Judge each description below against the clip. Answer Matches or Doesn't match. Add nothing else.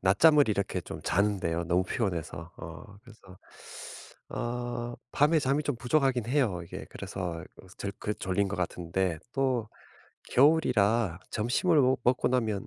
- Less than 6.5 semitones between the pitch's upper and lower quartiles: Matches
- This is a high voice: Doesn't match